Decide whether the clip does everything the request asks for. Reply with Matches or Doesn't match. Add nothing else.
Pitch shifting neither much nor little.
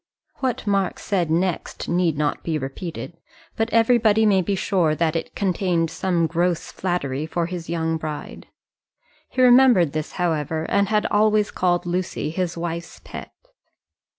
Matches